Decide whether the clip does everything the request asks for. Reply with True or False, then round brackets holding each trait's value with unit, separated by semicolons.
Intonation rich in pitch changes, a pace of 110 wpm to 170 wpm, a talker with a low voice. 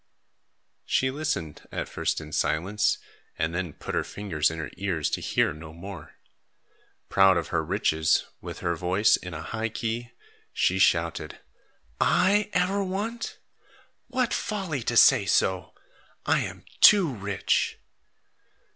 True (8.6 semitones; 140 wpm; 100 Hz)